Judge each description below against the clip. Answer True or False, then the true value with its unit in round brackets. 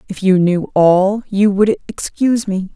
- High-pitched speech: True (200 Hz)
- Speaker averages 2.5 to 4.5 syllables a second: True (4.3 syllables/s)